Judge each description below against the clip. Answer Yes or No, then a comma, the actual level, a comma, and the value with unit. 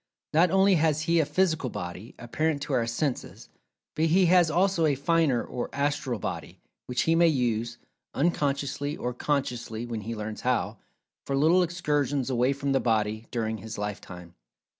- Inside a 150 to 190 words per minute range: Yes, average, 165 wpm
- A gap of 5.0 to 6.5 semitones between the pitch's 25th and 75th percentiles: Yes, wide, 5.4 semitones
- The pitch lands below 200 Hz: Yes, medium, 140 Hz